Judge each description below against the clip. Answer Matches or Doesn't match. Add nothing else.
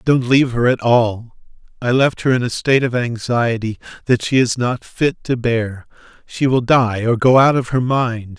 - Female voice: Doesn't match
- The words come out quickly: Matches